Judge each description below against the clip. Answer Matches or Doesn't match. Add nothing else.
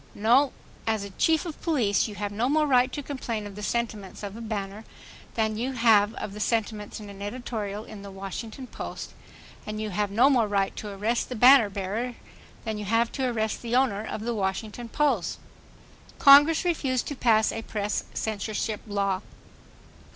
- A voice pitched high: Matches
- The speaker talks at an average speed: Matches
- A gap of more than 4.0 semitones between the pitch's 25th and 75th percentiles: Doesn't match